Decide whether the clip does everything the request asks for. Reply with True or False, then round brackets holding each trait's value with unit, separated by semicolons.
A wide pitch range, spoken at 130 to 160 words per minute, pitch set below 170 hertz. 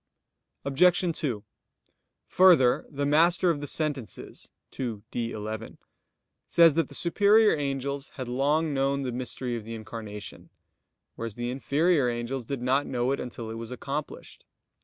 False (4.1 semitones; 145 wpm; 135 Hz)